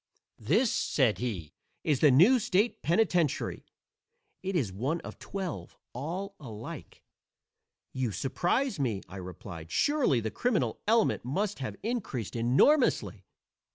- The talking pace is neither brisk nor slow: No, slow, 120 wpm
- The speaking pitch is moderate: Yes, medium, 145 Hz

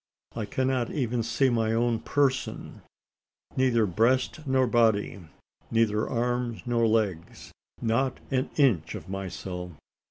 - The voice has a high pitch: No, low, 115 Hz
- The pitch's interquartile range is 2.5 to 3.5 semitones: Yes, average, 3.0 semitones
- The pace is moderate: No, slow, 120 wpm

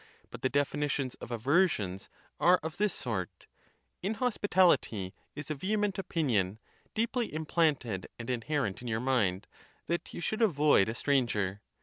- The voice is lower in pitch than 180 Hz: Yes, medium, 140 Hz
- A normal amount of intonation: No, wide, 7.9 semitones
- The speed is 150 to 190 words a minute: No, average, 140 wpm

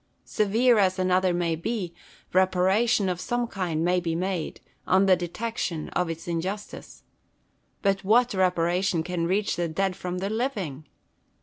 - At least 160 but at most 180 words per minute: No, average, 145 wpm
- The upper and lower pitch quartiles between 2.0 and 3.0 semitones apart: Yes, narrow, 2.5 semitones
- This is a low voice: No, medium, 185 Hz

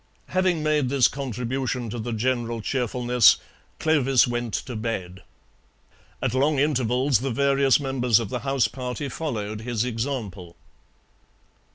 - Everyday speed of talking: No, slow, 130 wpm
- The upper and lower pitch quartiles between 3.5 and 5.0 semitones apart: No, average, 3.0 semitones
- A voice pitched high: No, low, 125 Hz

